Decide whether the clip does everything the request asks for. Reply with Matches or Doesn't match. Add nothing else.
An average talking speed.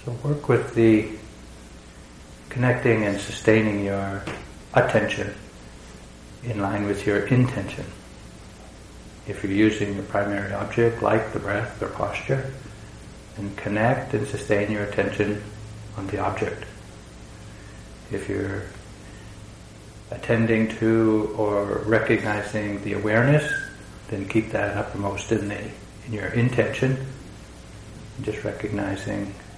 Doesn't match